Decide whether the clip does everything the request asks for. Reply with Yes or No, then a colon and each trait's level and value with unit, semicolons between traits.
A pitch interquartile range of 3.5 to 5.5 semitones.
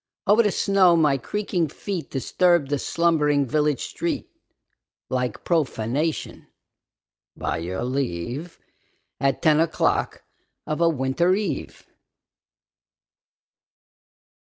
Yes: average, 4.4 semitones